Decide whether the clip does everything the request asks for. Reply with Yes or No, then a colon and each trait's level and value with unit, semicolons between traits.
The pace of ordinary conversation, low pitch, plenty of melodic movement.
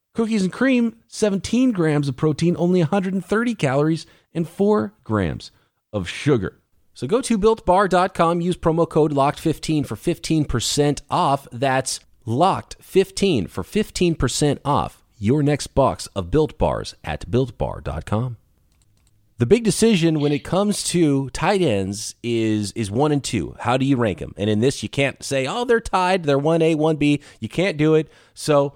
No: average, 170 wpm; medium, 155 Hz; wide, 6.5 semitones